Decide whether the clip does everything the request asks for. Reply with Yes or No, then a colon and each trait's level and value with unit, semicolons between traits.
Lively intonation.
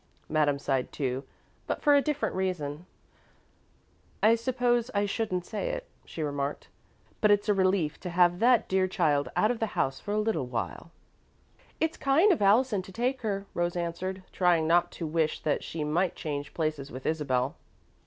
Yes: wide, 6.2 semitones